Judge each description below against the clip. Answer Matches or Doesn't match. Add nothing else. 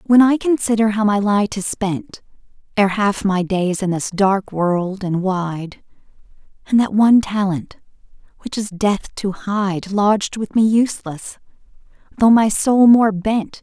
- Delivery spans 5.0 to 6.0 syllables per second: Doesn't match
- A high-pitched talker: Matches